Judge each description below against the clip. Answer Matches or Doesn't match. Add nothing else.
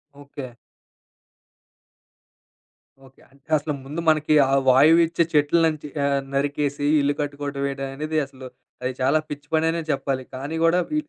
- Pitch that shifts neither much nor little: Doesn't match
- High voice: Doesn't match